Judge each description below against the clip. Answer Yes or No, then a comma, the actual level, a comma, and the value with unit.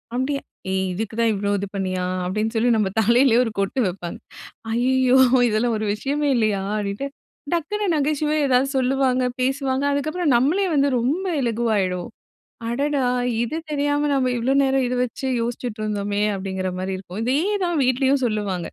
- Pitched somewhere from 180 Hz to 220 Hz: No, high, 245 Hz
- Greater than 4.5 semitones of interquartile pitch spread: Yes, average, 5.0 semitones